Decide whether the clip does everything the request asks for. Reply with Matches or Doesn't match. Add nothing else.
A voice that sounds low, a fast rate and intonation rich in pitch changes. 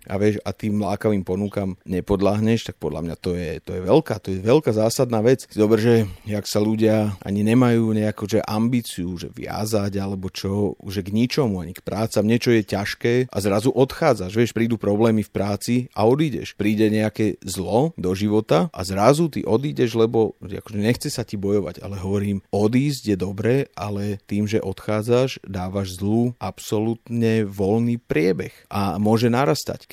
Doesn't match